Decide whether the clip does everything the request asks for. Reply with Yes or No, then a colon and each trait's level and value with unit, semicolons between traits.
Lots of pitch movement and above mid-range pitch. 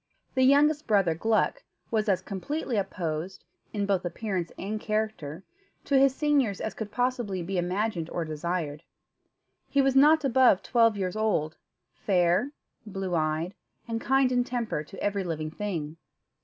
Yes: wide, 5.8 semitones; high, 205 Hz